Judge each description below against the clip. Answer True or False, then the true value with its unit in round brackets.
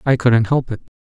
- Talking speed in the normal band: False (230 wpm)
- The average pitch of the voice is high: False (120 Hz)